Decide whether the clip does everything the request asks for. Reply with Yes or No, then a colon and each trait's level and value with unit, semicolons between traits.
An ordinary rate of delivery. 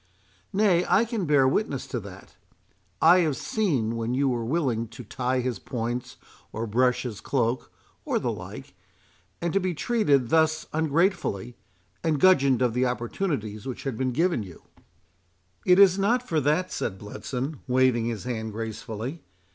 Yes: average, 155 wpm